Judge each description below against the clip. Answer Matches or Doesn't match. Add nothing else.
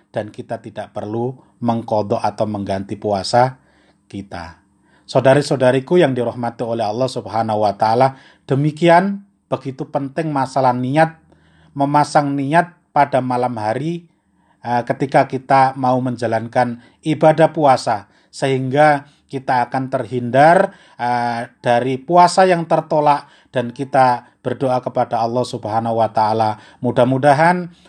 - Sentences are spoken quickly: Doesn't match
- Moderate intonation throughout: Matches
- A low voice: Matches